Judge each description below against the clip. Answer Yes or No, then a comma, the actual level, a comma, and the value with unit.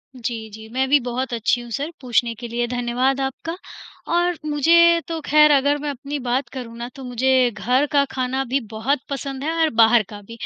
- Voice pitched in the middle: No, very high, 260 Hz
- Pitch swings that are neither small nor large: Yes, average, 3.2 semitones